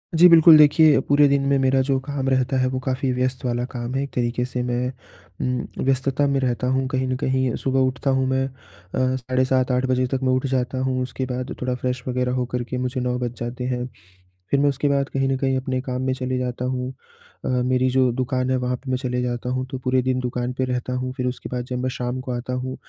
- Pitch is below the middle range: Yes, low, 130 Hz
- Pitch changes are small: Yes, narrow, 0.9 semitones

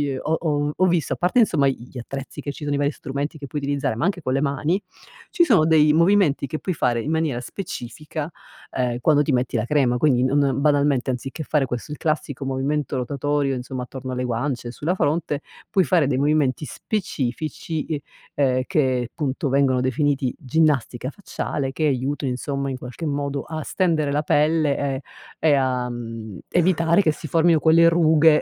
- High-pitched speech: No, medium, 145 Hz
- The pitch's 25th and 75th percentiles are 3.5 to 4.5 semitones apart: No, average, 3.1 semitones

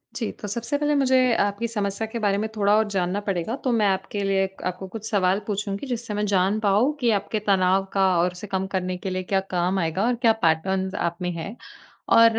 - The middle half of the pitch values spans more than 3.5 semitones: No, average, 2.8 semitones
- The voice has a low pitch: No, high, 200 Hz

